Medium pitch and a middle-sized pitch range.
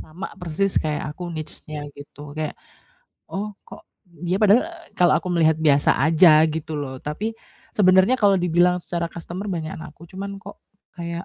Yes: medium, 170 Hz; average, 3.4 semitones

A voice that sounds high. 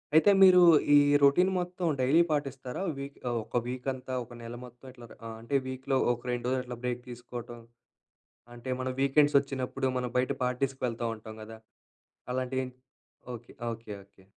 No: low, 125 Hz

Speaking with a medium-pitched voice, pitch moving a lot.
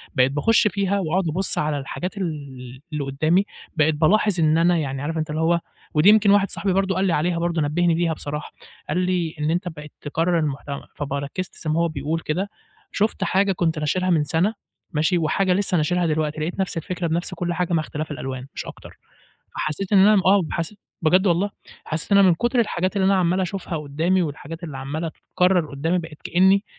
No: medium, 170 Hz; average, 3.6 semitones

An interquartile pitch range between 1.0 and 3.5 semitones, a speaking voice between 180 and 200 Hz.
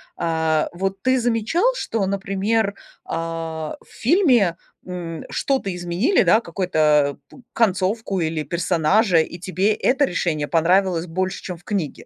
No: average, 4.5 semitones; medium, 185 Hz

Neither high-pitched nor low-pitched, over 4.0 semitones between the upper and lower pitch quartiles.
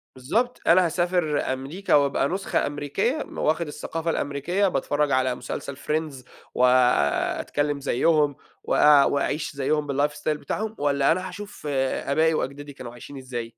No: medium, 145 Hz; average, 3.2 semitones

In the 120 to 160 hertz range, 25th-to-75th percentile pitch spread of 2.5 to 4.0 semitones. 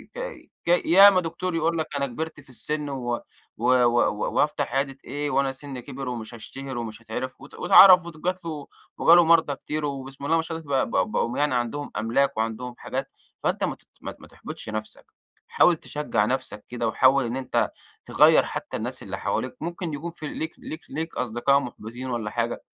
No: medium, 140 Hz; average, 4.7 semitones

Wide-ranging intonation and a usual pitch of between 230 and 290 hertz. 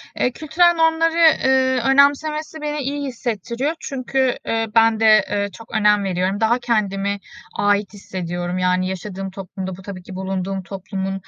No: wide, 5.9 semitones; high, 210 Hz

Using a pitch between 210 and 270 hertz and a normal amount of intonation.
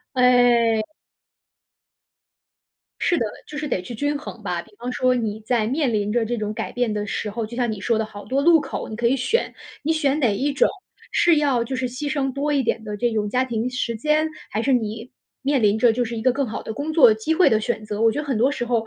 Yes: high, 240 Hz; average, 3.9 semitones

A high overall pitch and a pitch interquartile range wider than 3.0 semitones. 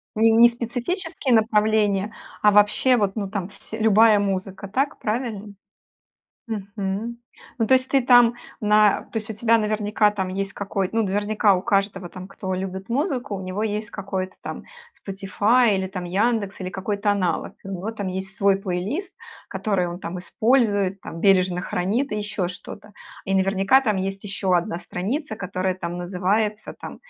No: high, 205 Hz; narrow, 2.6 semitones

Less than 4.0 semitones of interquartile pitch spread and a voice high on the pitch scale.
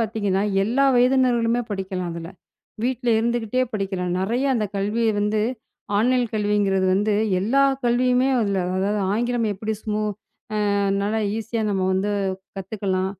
Yes: average, 3.4 semitones; high, 215 Hz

